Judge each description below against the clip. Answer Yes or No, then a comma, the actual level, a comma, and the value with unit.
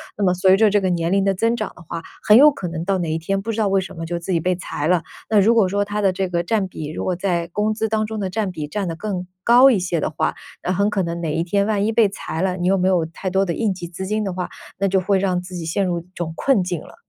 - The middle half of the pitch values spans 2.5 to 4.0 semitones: Yes, average, 2.9 semitones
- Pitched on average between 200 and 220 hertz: No, high, 190 Hz